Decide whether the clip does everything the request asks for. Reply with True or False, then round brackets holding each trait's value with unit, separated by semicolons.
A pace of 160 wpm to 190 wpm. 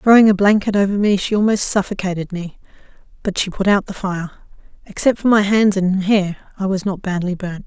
False (205 wpm)